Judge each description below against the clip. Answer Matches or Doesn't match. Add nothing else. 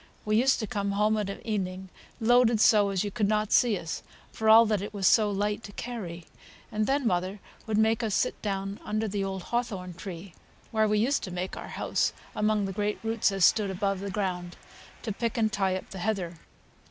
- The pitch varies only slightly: Matches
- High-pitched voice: Matches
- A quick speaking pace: Matches